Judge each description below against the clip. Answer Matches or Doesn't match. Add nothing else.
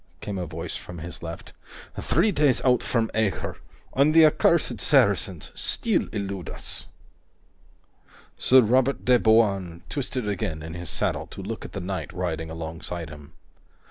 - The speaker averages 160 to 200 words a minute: Doesn't match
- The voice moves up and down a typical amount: Doesn't match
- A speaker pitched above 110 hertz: Doesn't match